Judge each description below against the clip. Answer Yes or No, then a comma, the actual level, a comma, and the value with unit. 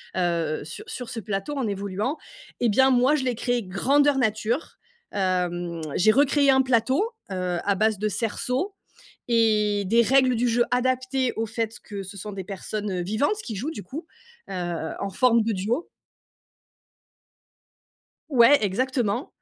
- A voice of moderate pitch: No, high, 225 Hz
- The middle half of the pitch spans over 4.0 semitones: Yes, average, 4.7 semitones